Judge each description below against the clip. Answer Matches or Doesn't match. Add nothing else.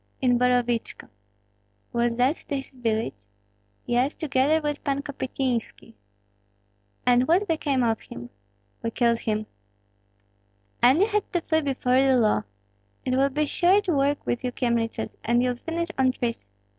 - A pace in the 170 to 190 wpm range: Doesn't match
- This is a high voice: Matches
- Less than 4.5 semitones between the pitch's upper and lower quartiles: Matches